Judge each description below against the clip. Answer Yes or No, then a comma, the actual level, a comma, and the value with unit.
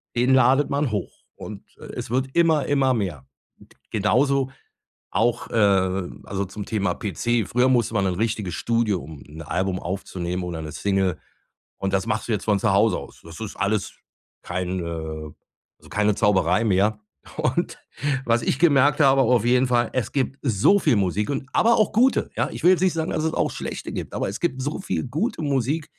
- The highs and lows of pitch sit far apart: Yes, wide, 5.7 semitones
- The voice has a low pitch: Yes, low, 110 Hz